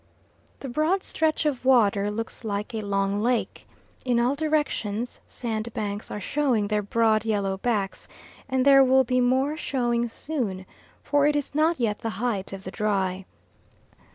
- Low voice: No, high, 235 Hz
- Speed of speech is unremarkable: Yes, average, 155 wpm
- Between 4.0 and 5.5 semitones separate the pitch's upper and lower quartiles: Yes, average, 4.4 semitones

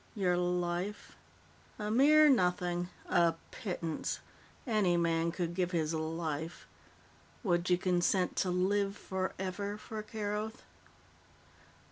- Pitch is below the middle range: No, medium, 180 Hz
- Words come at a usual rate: No, slow, 105 wpm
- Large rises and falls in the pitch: No, average, 3.0 semitones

